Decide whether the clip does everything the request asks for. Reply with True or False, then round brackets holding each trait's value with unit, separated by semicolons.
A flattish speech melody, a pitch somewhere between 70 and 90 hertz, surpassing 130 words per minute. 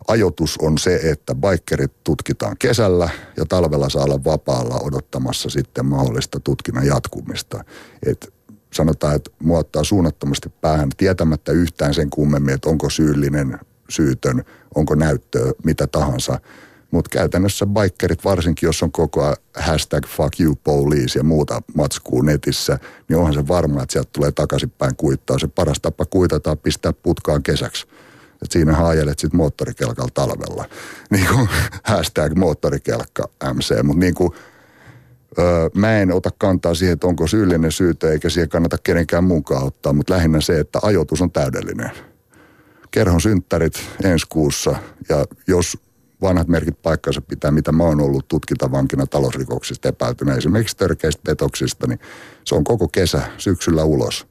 False (3.4 semitones; 80 Hz; 145 wpm)